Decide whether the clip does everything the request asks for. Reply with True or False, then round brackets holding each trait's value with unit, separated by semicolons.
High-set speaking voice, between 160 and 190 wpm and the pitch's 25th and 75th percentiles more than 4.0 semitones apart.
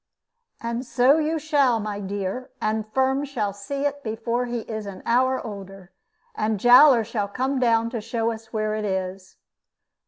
False (230 Hz; 165 wpm; 3.6 semitones)